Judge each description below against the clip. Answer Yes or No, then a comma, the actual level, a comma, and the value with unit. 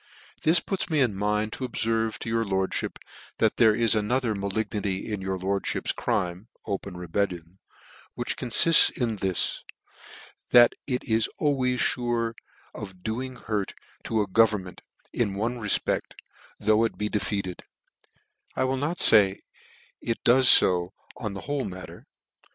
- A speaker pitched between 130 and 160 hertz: No, low, 110 Hz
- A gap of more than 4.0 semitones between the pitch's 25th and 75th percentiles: No, average, 3.6 semitones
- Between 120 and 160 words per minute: Yes, average, 145 wpm